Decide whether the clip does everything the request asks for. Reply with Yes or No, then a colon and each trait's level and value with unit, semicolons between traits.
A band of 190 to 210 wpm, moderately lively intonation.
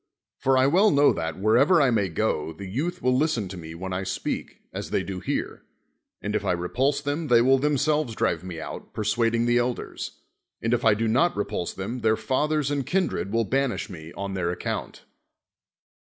No: fast, 205 wpm; wide, 6.5 semitones